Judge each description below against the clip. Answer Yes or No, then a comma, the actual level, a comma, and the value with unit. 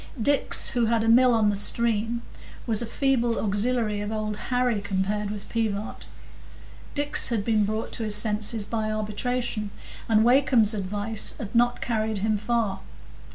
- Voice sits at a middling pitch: No, high, 220 Hz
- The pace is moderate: Yes, average, 155 wpm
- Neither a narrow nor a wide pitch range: No, narrow, 2.1 semitones